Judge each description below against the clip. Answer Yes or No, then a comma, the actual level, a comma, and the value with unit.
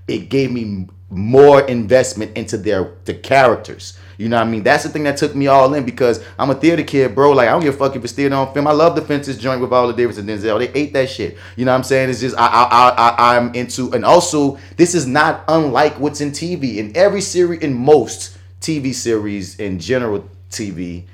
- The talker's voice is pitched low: Yes, low, 130 Hz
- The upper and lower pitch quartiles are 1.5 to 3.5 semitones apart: No, average, 4.7 semitones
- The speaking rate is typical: No, fast, 240 wpm